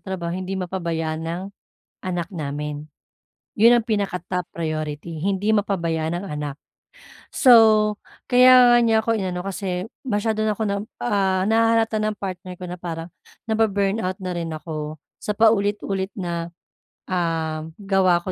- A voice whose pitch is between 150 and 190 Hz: Yes, medium, 185 Hz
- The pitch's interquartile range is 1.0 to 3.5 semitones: No, average, 4.0 semitones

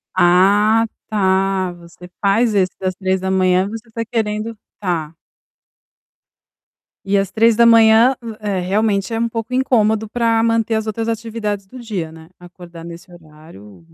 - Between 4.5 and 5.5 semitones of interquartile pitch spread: No, average, 3.7 semitones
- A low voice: No, high, 205 Hz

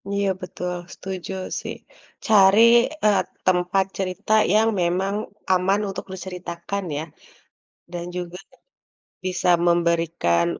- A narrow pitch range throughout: Yes, narrow, 2.0 semitones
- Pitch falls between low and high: Yes, medium, 180 Hz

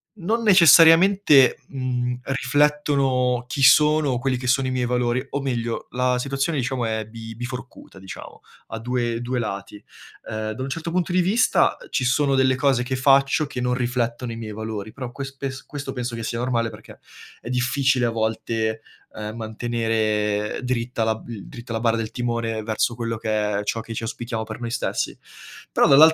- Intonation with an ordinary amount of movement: Yes, average, 3.1 semitones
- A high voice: No, low, 125 Hz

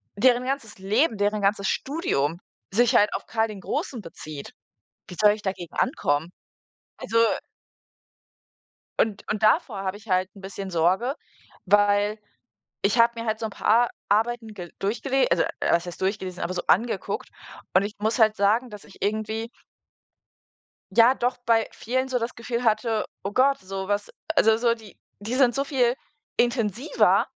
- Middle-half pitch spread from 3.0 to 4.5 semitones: Yes, average, 3.4 semitones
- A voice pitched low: No, high, 215 Hz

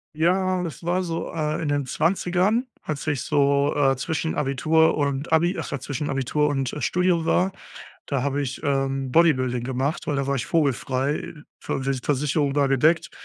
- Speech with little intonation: No, average, 3.2 semitones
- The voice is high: No, medium, 145 Hz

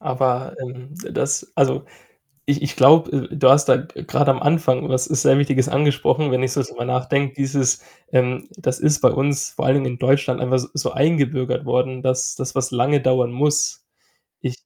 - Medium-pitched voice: No, low, 130 Hz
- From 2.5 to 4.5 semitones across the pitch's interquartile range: No, narrow, 2.0 semitones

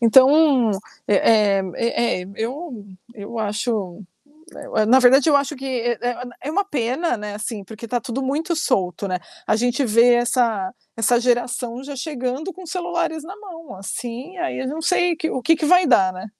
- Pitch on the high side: Yes, high, 245 Hz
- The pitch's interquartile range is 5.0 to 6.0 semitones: Yes, average, 5.3 semitones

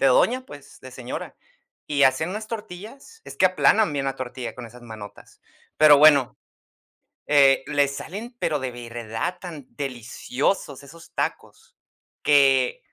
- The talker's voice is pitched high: No, medium, 140 Hz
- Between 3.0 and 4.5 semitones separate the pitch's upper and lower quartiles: No, average, 5.0 semitones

